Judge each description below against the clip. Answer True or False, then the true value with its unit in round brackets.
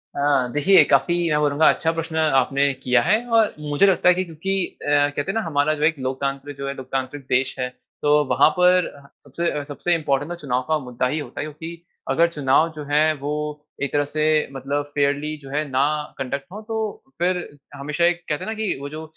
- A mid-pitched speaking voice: True (145 Hz)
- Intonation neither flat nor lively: True (3.0 semitones)